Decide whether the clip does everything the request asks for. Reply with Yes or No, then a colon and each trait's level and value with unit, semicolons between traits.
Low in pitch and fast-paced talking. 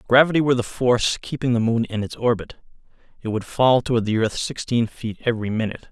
Yes: low, 120 Hz; fast, 215 wpm